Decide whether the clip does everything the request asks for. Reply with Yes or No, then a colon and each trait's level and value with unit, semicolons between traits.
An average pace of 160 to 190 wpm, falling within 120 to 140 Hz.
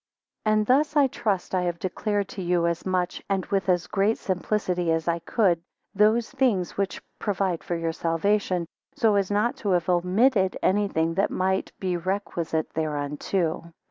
No: average, 170 wpm; medium, 185 Hz